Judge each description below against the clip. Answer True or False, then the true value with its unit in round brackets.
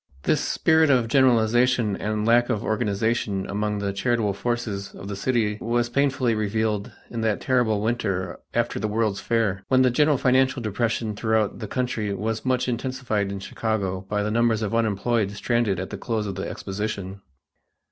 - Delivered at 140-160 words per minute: False (170 wpm)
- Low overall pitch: True (110 Hz)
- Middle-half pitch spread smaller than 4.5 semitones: True (2.9 semitones)